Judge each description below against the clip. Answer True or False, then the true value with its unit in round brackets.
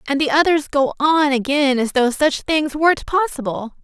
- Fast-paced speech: False (190 wpm)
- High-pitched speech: True (285 Hz)